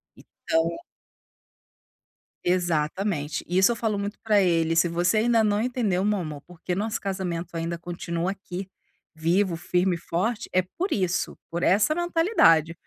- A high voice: No, medium, 180 Hz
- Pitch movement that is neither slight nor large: Yes, average, 3.7 semitones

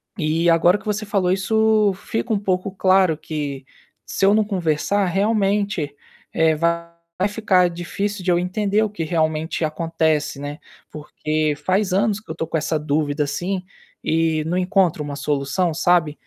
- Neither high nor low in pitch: Yes, medium, 175 Hz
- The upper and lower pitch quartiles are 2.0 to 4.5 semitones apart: Yes, average, 4.1 semitones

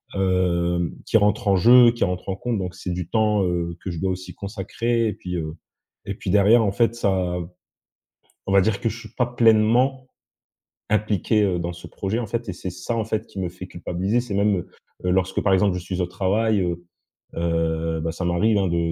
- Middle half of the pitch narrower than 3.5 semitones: No, average, 3.8 semitones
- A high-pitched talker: No, very low, 95 Hz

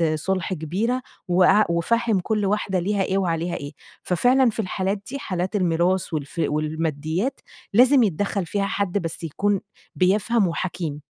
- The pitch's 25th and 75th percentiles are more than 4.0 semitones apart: No, average, 3.6 semitones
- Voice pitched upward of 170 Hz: Yes, medium, 185 Hz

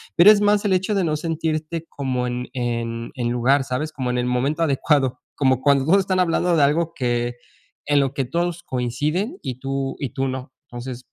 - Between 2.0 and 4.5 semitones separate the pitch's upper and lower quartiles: No, average, 4.9 semitones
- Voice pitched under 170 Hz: Yes, medium, 140 Hz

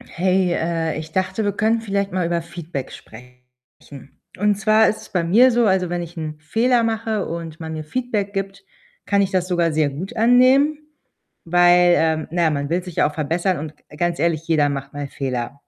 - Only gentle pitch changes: No, average, 4.1 semitones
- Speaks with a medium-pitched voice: Yes, medium, 175 Hz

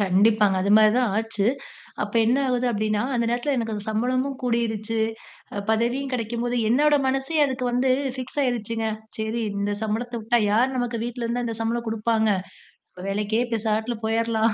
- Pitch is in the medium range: No, high, 230 Hz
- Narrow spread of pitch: Yes, narrow, 2.0 semitones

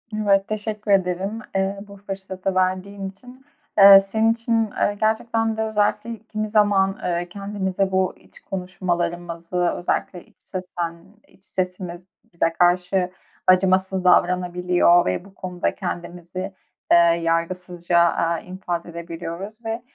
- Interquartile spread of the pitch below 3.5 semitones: Yes, narrow, 2.4 semitones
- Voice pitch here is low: No, medium, 185 Hz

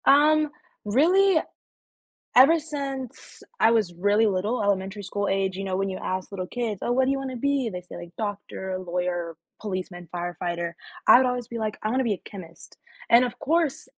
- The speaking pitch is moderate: No, high, 210 Hz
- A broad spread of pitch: Yes, wide, 5.9 semitones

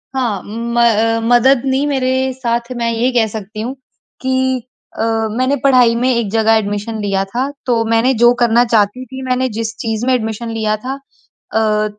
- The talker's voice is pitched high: Yes, high, 235 Hz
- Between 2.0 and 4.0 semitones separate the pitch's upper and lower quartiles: Yes, narrow, 2.5 semitones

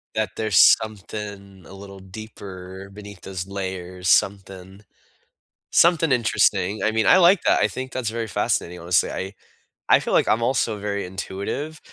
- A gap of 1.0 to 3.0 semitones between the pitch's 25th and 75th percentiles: Yes, average, 2.7 semitones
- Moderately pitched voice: No, low, 100 Hz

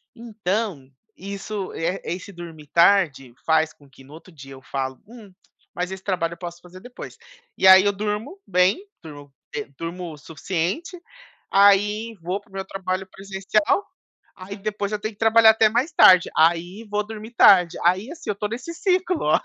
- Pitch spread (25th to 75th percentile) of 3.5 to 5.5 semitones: Yes, average, 3.9 semitones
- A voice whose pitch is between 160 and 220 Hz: Yes, high, 190 Hz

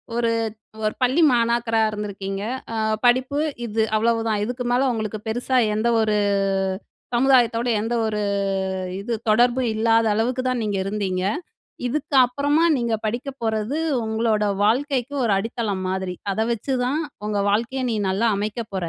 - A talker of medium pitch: No, high, 230 Hz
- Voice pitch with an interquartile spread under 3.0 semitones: Yes, narrow, 2.6 semitones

